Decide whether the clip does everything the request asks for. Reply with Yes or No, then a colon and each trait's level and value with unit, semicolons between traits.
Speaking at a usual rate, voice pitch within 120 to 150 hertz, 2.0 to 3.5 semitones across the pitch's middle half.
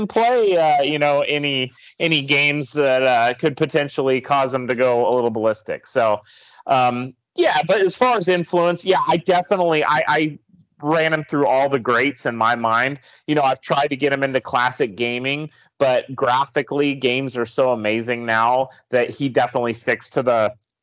No: average, 180 wpm; medium, 140 Hz; average, 3.9 semitones